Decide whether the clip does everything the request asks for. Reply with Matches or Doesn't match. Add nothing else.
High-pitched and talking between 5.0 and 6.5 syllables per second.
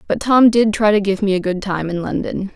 Matches